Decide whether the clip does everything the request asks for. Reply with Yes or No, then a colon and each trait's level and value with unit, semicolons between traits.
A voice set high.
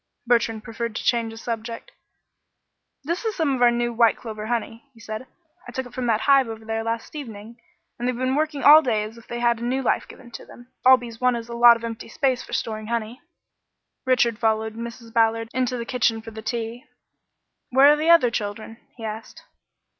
Yes: high, 235 Hz